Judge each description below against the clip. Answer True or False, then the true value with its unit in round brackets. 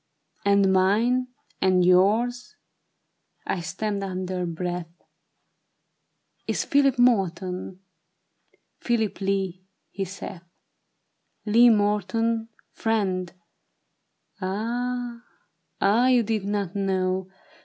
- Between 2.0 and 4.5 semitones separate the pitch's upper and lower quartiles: True (3.5 semitones)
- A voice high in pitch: True (200 Hz)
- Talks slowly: True (95 wpm)